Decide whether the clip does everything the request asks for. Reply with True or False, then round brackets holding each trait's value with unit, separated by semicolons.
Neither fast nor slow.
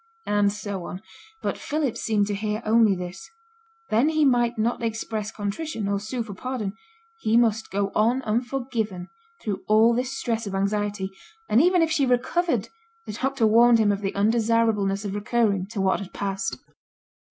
True (170 wpm)